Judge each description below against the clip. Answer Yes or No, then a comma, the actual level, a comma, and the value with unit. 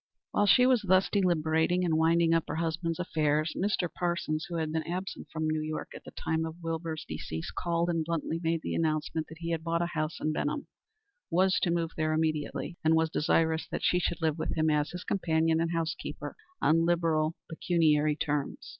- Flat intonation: Yes, narrow, 1.5 semitones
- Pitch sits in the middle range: Yes, medium, 165 Hz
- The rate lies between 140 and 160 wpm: No, average, 200 wpm